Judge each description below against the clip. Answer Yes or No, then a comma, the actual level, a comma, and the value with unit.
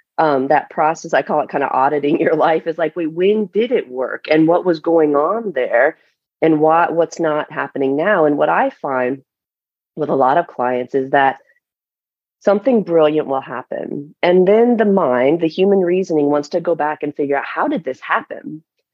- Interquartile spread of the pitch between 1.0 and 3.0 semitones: No, average, 3.7 semitones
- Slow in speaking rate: No, average, 200 wpm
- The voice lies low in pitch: No, medium, 160 Hz